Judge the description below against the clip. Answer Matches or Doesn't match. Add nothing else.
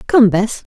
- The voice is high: Matches